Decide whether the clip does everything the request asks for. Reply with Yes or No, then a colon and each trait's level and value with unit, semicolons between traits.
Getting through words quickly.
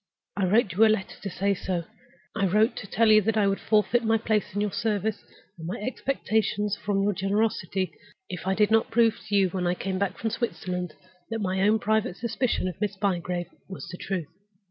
Yes: fast, 210 wpm